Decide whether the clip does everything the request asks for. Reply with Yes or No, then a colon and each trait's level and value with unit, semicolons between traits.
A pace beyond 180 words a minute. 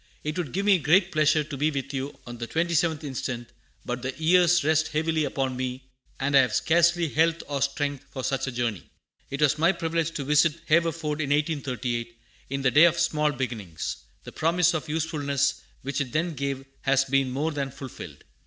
Yes: average, 195 wpm